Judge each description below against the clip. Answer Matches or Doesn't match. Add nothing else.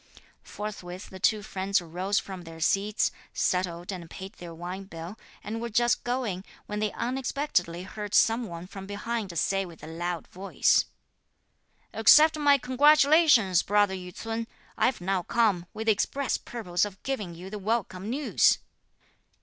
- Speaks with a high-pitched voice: Matches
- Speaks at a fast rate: Doesn't match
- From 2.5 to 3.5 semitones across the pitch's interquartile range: Doesn't match